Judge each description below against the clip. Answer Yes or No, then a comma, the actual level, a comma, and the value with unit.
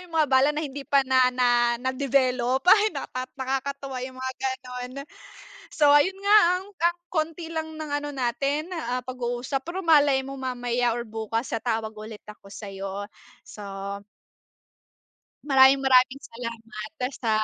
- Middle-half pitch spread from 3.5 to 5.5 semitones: No, average, 3.1 semitones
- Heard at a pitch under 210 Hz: No, very high, 260 Hz